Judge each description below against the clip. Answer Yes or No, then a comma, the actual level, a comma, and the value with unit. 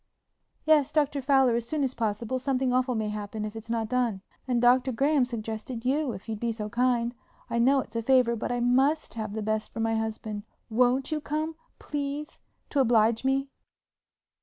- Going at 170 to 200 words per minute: Yes, average, 190 wpm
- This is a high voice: Yes, high, 245 Hz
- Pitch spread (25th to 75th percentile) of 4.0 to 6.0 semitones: No, average, 3.2 semitones